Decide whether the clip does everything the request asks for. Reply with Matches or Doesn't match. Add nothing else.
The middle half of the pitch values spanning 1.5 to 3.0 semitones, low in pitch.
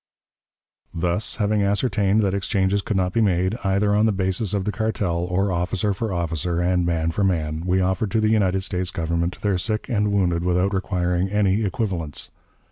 Matches